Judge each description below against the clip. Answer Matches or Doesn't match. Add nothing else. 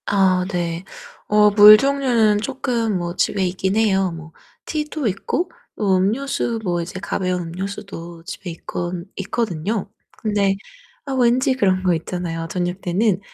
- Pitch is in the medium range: Doesn't match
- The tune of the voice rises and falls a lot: Doesn't match